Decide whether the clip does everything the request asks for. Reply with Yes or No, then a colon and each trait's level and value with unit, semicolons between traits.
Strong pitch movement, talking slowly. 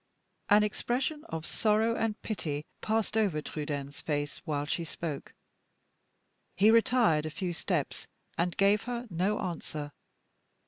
Yes: wide, 6.3 semitones; slow, 130 wpm